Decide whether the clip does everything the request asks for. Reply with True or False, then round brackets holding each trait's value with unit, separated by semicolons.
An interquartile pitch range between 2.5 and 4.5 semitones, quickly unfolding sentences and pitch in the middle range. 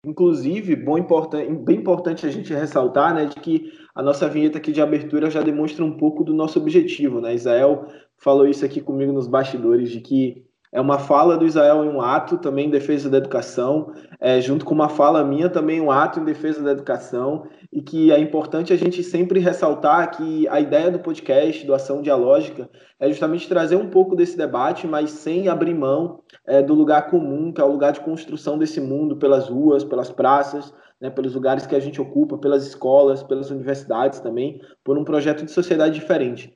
True (3.3 semitones; 200 wpm; 150 Hz)